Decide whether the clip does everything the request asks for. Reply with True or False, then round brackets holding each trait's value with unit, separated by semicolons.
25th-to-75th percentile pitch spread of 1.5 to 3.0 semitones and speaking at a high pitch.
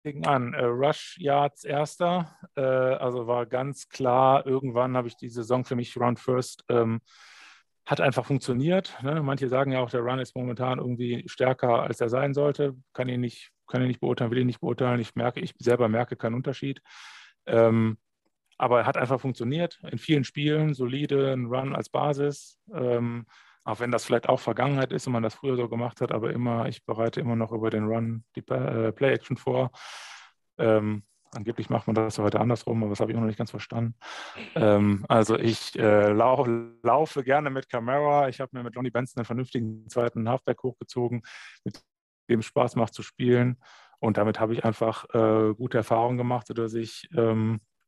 False (2.4 semitones; 125 Hz)